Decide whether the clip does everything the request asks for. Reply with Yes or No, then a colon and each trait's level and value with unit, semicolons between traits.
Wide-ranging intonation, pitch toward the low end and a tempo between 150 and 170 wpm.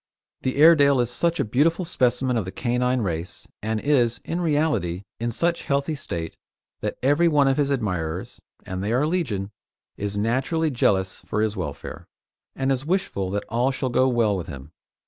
No: wide, 6.2 semitones; low, 125 Hz; average, 180 wpm